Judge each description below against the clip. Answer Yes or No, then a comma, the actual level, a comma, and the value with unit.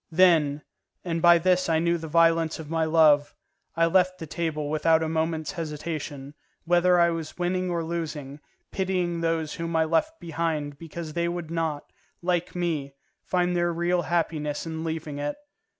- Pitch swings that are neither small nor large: No, narrow, 1.7 semitones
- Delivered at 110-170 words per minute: Yes, average, 165 wpm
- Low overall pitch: No, medium, 165 Hz